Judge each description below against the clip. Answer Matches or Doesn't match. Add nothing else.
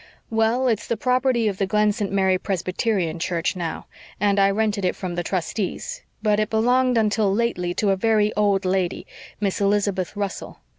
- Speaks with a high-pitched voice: Matches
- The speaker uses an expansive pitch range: Doesn't match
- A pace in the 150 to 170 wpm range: Doesn't match